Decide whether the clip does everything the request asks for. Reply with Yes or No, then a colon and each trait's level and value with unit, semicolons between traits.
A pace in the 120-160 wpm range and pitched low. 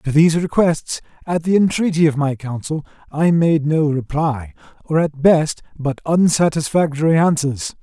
No: average, 145 wpm; medium, 155 Hz